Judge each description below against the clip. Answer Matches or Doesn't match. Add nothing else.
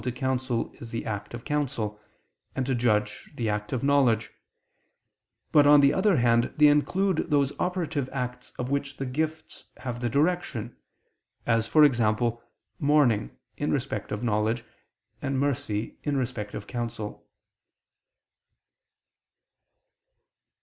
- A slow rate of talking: Matches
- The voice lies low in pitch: Matches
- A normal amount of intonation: Matches